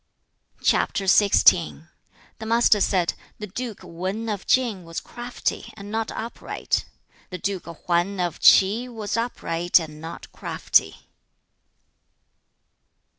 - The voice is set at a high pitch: Yes, high, 195 Hz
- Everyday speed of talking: No, slow, 115 wpm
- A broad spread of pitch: No, average, 4.4 semitones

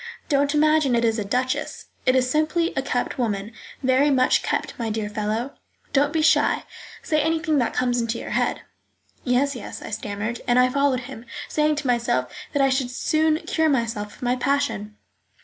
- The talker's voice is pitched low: No, very high, 255 Hz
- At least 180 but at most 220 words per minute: Yes, average, 185 wpm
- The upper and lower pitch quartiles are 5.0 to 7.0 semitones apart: No, average, 3.7 semitones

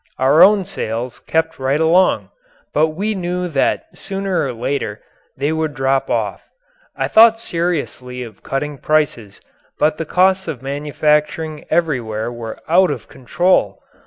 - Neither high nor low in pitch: Yes, medium, 150 Hz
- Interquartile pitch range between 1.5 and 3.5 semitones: No, average, 4.9 semitones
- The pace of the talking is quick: No, average, 140 wpm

